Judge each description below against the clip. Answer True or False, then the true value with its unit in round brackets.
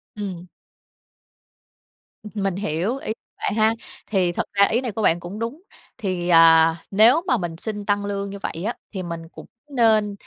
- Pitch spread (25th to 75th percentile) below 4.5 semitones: True (3.9 semitones)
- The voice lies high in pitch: True (200 Hz)